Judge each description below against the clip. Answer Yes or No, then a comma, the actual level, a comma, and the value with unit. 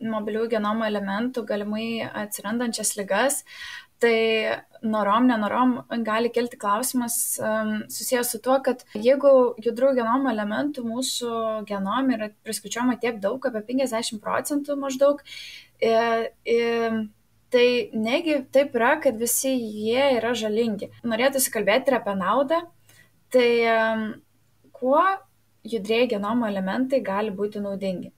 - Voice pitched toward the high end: Yes, high, 235 Hz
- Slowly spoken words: Yes, slow, 110 wpm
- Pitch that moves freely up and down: No, average, 3.0 semitones